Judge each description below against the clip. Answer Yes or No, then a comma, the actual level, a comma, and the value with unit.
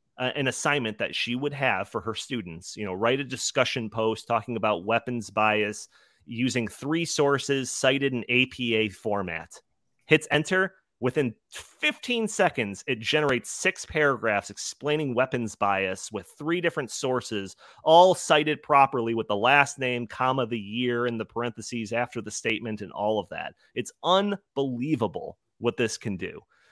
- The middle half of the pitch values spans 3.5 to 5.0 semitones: Yes, average, 4.3 semitones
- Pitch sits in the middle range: No, low, 125 Hz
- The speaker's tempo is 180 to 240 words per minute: No, average, 155 wpm